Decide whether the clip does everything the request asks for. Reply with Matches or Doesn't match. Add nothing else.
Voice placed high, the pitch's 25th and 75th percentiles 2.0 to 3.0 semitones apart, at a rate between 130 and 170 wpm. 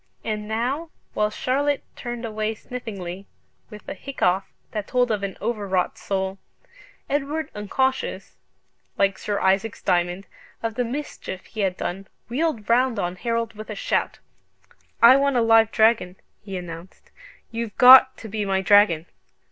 Doesn't match